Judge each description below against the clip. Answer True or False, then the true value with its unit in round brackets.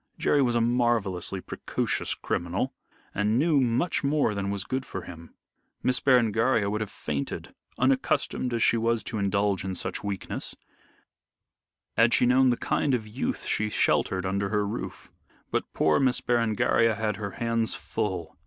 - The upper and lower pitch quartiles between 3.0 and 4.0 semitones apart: True (3.7 semitones)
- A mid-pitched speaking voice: False (110 Hz)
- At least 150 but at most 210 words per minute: True (160 wpm)